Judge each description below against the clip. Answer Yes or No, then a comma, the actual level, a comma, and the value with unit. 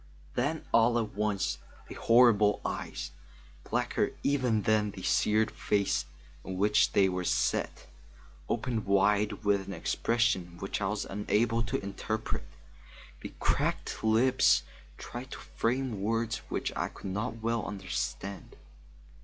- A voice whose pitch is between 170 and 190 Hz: No, low, 105 Hz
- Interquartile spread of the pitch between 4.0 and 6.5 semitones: No, narrow, 2.6 semitones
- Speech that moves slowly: Yes, slow, 130 wpm